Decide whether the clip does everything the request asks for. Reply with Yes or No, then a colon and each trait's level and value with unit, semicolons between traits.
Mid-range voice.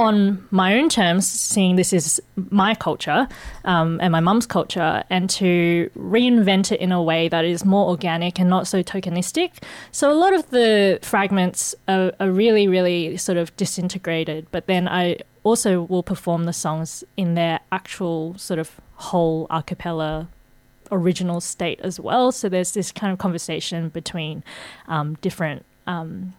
Yes: medium, 180 Hz